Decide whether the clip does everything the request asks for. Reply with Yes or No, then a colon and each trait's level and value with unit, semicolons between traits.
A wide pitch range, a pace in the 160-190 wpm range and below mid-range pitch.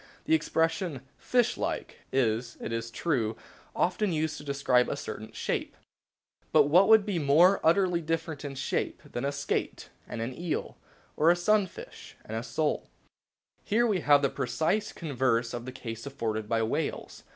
No: wide, 6.2 semitones; average, 165 wpm; medium, 145 Hz